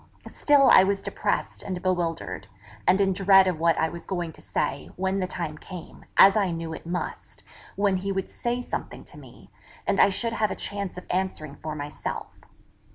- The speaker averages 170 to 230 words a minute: Yes, average, 195 wpm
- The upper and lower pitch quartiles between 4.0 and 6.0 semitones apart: No, average, 2.9 semitones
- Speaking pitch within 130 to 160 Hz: No, medium, 185 Hz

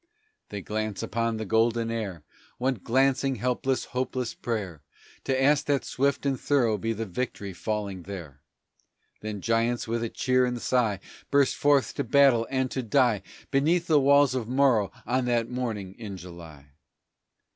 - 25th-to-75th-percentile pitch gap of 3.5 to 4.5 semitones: Yes, average, 3.8 semitones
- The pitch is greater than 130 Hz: No, low, 120 Hz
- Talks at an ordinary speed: Yes, average, 155 wpm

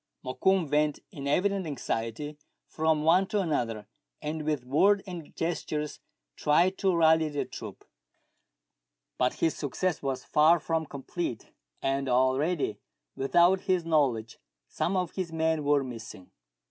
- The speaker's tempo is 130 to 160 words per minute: Yes, slow, 135 wpm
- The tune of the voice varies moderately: Yes, average, 4.0 semitones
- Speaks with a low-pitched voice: No, medium, 155 Hz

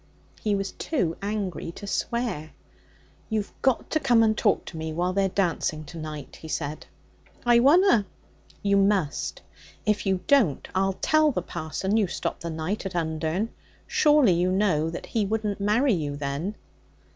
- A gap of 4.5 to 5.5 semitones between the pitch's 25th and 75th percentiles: Yes, average, 5.2 semitones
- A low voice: No, high, 195 Hz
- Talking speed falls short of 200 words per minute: Yes, average, 165 wpm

